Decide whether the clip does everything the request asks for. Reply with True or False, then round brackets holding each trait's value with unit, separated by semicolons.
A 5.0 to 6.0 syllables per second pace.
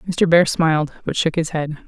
True (5.1 syllables/s)